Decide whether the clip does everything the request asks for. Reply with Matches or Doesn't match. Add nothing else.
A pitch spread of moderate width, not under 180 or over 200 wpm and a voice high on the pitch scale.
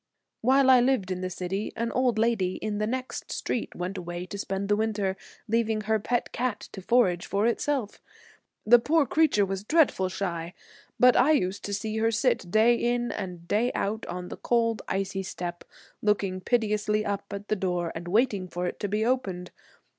Matches